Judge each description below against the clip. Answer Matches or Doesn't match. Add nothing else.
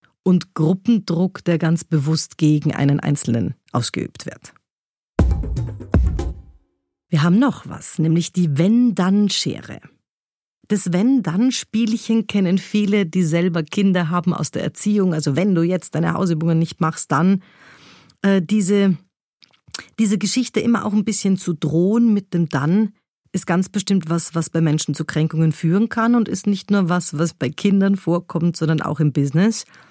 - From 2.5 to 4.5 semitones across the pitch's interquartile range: Matches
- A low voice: Doesn't match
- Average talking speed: Matches